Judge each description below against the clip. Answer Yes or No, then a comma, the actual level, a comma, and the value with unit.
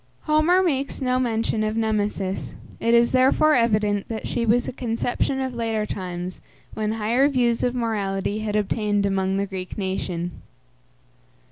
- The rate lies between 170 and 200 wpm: No, average, 150 wpm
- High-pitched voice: Yes, high, 220 Hz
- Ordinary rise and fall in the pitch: Yes, average, 3.5 semitones